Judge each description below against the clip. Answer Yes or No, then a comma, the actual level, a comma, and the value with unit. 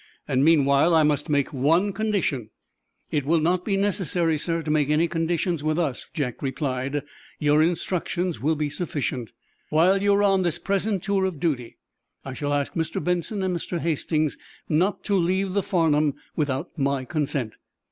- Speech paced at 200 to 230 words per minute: No, average, 165 wpm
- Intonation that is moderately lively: Yes, average, 3.9 semitones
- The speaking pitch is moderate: Yes, medium, 160 Hz